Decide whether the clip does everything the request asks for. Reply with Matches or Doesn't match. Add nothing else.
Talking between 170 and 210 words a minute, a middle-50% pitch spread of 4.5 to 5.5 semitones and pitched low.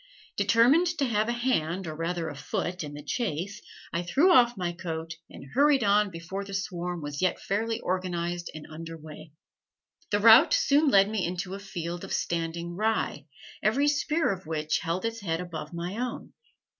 Doesn't match